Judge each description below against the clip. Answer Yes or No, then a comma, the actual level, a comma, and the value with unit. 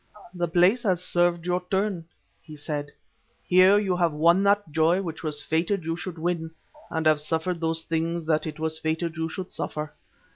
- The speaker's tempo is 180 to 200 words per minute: Yes, average, 190 wpm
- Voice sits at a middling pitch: Yes, medium, 165 Hz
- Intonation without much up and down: Yes, narrow, 2.0 semitones